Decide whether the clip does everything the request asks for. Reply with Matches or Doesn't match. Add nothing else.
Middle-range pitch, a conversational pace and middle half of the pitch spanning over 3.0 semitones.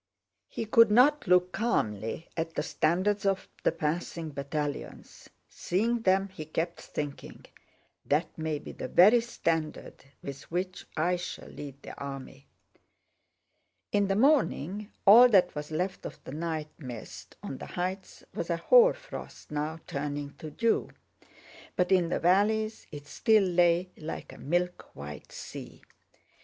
Matches